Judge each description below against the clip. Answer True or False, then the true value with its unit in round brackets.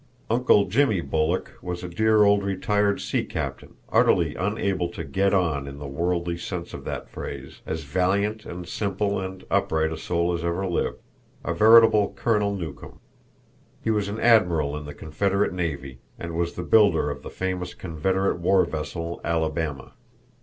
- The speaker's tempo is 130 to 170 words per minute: True (165 wpm)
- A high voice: False (90 Hz)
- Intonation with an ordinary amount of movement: True (3.7 semitones)